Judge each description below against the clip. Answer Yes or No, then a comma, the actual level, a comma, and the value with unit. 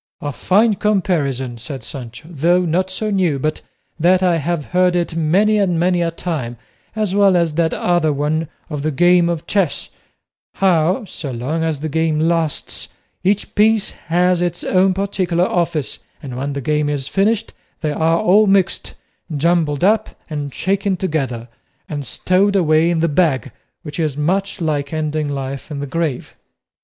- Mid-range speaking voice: Yes, medium, 165 Hz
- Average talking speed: Yes, average, 170 wpm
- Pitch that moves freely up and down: No, average, 3.8 semitones